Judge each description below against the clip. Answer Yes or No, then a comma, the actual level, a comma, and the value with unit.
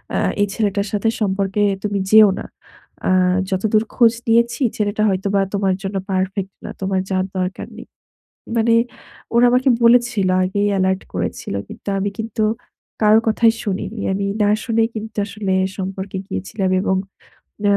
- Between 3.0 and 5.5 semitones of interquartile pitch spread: No, narrow, 2.6 semitones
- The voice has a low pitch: No, high, 205 Hz